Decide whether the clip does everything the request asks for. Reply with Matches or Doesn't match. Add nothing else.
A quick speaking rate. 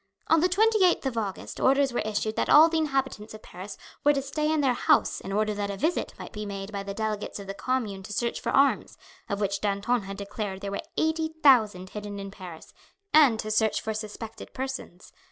Matches